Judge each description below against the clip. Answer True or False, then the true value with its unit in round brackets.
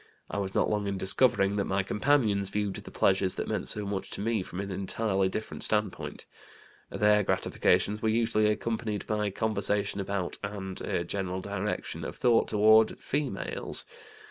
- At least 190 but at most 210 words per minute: False (165 wpm)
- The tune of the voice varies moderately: False (1.8 semitones)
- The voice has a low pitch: True (105 Hz)